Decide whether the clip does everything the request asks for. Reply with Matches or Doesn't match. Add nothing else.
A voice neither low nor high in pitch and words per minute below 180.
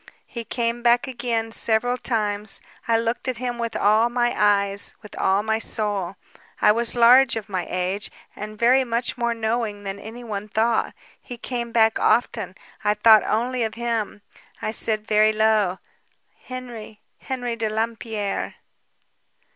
Doesn't match